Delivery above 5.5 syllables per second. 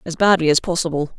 Yes: 6.4 syllables/s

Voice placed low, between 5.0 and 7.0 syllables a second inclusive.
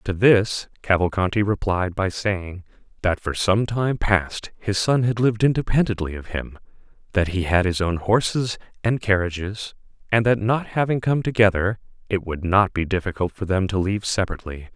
Yes: low, 100 Hz; 5.1 syllables/s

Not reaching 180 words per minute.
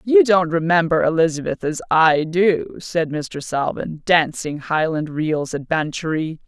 Yes: average, 140 wpm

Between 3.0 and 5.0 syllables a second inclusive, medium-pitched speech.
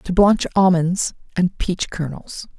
Yes: 3.7 syllables/s; medium, 180 Hz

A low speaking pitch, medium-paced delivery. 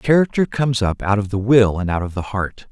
No: low, 110 Hz; fast, 265 wpm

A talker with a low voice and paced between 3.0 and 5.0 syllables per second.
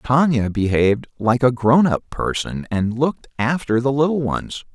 Yes: low, 125 Hz; 4.6 syllables/s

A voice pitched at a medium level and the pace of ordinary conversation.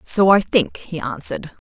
Yes: medium, 170 Hz; average, 180 wpm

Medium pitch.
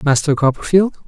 Yes: medium, 155 Hz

